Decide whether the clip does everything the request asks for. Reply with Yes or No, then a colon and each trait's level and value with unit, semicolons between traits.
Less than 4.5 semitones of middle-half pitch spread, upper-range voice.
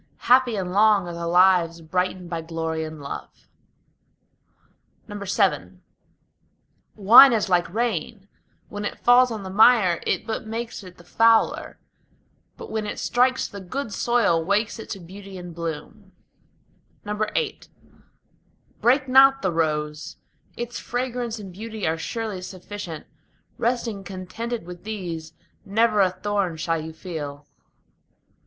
No: average, 4.9 semitones; high, 195 Hz